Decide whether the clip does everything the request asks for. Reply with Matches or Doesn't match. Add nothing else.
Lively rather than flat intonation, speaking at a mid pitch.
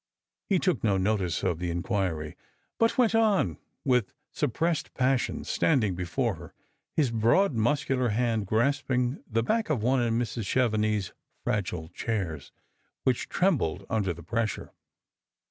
Doesn't match